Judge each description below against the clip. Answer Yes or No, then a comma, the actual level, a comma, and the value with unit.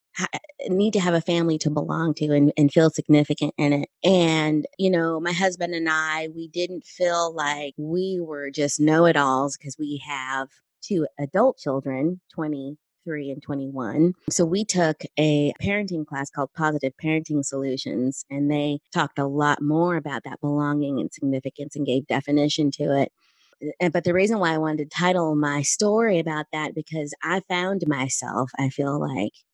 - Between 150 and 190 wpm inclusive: Yes, average, 175 wpm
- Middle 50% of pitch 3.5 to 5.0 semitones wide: No, average, 2.9 semitones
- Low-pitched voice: No, medium, 150 Hz